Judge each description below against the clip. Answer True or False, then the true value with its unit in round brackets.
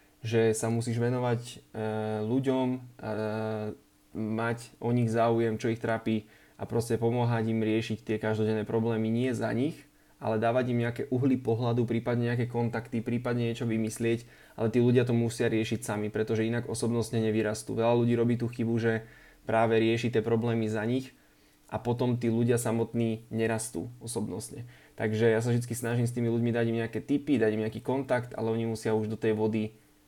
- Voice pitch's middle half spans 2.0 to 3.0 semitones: False (1.3 semitones)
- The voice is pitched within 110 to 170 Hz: True (115 Hz)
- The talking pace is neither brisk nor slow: False (175 wpm)